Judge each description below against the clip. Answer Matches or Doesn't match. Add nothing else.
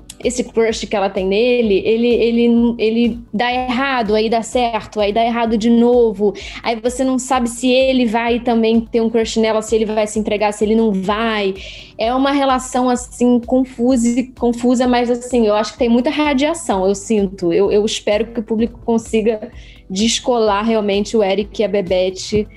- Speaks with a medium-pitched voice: Doesn't match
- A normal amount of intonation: Doesn't match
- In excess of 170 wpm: Matches